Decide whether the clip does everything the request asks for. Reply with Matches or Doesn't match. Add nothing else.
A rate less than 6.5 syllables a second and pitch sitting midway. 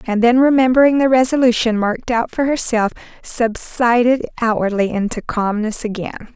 Doesn't match